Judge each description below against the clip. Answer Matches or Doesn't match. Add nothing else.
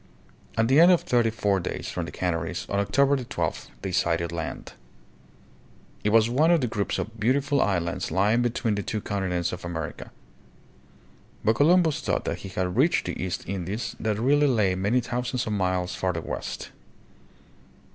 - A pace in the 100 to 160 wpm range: Doesn't match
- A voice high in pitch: Doesn't match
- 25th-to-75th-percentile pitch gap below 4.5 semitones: Doesn't match